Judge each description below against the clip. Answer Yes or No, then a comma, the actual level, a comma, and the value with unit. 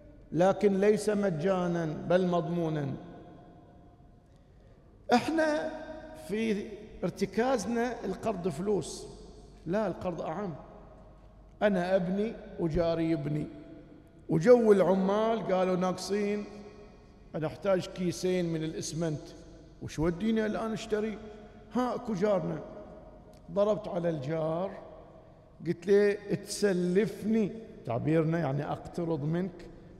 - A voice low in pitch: No, high, 190 Hz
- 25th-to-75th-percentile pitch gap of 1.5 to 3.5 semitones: No, average, 3.9 semitones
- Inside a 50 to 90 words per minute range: Yes, average, 85 wpm